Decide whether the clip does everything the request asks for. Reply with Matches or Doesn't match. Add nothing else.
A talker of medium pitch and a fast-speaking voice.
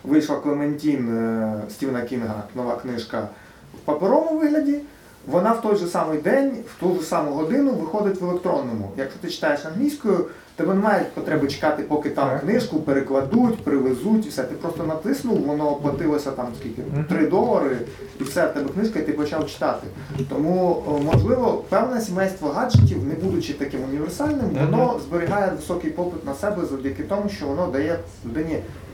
Matches